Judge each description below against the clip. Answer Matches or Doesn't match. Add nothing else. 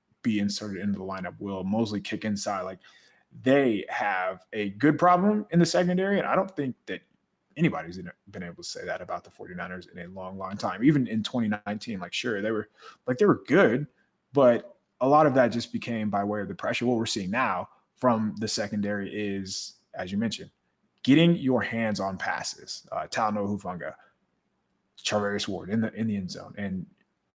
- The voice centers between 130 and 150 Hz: Doesn't match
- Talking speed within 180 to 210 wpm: Matches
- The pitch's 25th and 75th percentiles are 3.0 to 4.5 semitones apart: Matches